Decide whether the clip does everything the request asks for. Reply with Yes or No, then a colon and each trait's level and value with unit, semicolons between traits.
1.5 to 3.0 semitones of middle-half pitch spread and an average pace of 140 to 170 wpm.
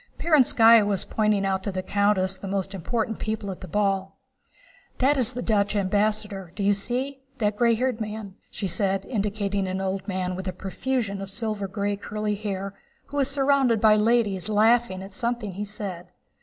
No: narrow, 2.6 semitones; average, 185 wpm